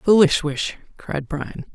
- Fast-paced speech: No, average, 170 wpm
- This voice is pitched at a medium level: Yes, medium, 165 Hz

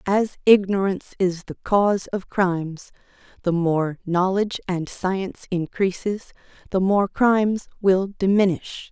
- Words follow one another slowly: Yes, slow, 120 wpm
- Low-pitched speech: No, high, 190 Hz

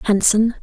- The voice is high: Yes, high, 215 Hz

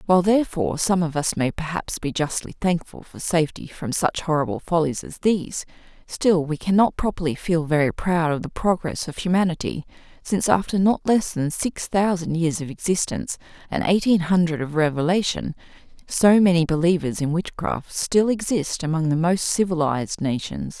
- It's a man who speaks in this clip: No, female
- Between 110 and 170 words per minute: Yes, average, 165 wpm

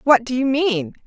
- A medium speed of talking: No, fast, 225 wpm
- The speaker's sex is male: No, female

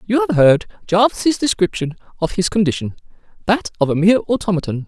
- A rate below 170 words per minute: Yes, average, 160 wpm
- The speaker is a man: Yes, male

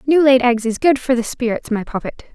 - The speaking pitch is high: Yes, very high, 250 Hz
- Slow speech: No, fast, 255 wpm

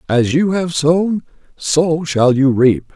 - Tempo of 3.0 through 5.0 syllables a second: Yes, 3.3 syllables/s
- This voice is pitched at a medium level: Yes, medium, 150 Hz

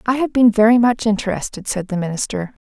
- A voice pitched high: Yes, high, 220 Hz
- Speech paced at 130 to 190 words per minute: No, average, 200 wpm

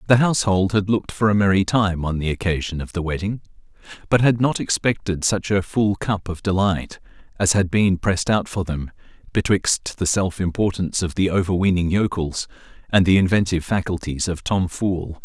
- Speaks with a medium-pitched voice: No, very low, 95 Hz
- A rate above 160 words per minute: Yes, average, 180 wpm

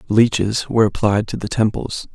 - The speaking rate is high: No, average, 170 wpm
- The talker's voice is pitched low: Yes, low, 110 Hz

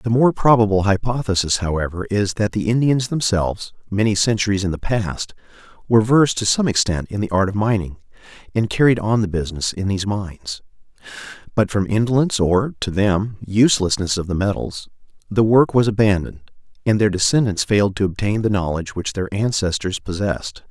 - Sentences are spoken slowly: No, average, 170 wpm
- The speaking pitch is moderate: No, low, 100 Hz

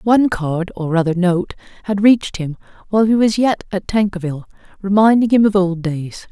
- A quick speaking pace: No, average, 180 wpm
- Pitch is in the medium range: No, high, 195 Hz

